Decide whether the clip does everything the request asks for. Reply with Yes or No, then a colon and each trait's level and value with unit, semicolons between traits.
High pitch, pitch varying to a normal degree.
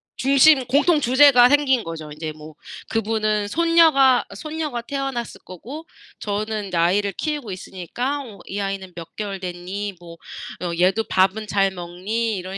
No: high, 210 Hz; wide, 6.2 semitones